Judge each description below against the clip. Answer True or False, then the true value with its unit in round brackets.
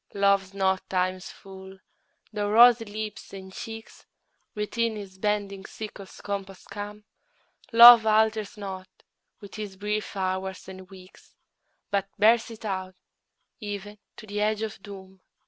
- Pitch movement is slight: True (2.0 semitones)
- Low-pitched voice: False (200 Hz)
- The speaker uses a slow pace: True (130 wpm)